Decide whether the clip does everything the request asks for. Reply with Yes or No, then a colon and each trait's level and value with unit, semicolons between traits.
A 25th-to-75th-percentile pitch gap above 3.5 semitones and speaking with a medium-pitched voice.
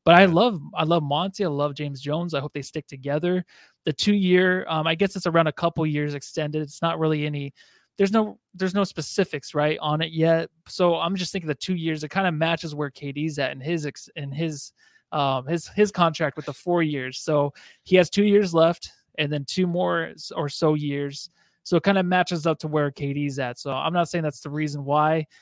No: average, 3.0 semitones; medium, 160 Hz